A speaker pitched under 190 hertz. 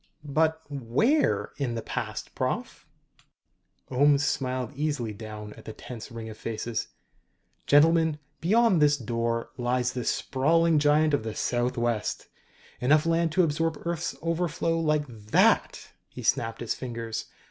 Yes: medium, 140 Hz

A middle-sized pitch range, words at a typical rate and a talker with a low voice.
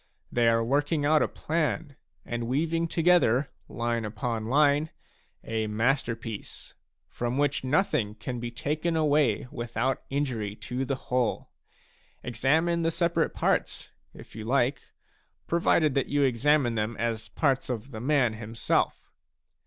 No: average, 4.4 semitones; slow, 130 wpm; low, 130 Hz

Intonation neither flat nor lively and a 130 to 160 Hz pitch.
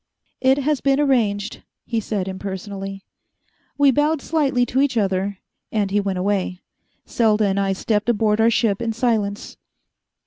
No: average, 4.2 semitones; high, 215 Hz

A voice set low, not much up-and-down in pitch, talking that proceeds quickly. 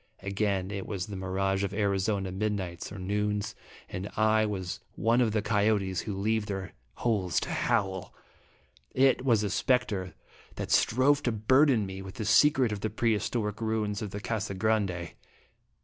No: low, 105 Hz; narrow, 2.2 semitones; average, 165 wpm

